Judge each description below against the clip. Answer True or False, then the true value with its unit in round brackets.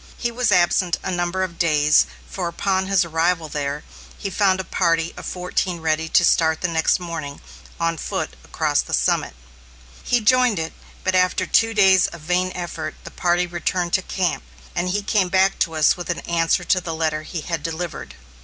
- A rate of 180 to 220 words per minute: True (190 wpm)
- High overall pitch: False (175 Hz)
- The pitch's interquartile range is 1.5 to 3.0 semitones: True (2.4 semitones)